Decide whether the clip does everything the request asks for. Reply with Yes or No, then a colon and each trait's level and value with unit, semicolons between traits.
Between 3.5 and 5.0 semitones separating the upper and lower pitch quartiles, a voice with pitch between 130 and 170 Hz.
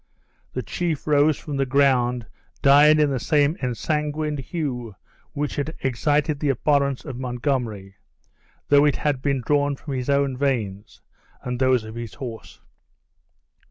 No: average, 2.9 semitones; medium, 140 Hz